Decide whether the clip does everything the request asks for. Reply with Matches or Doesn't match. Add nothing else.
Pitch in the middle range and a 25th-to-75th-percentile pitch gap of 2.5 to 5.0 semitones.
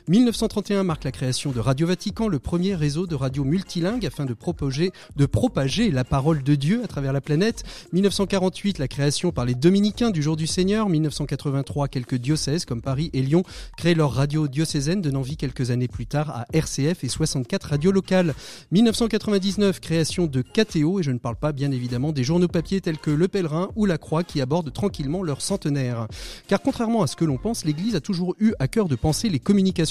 Doesn't match